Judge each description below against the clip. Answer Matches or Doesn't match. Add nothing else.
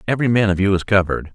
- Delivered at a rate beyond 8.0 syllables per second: Matches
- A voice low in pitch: Matches